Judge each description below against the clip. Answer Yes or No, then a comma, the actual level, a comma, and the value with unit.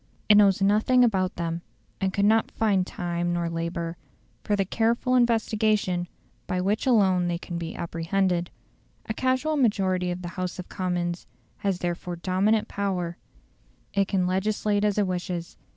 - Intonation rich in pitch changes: No, average, 3.1 semitones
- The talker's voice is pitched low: No, medium, 185 Hz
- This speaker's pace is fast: No, average, 155 wpm